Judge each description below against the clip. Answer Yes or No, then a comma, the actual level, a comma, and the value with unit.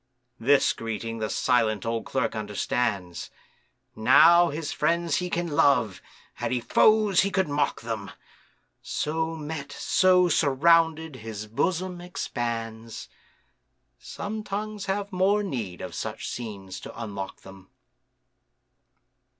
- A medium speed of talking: No, slow, 120 wpm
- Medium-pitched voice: Yes, medium, 145 Hz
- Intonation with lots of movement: Yes, wide, 7.6 semitones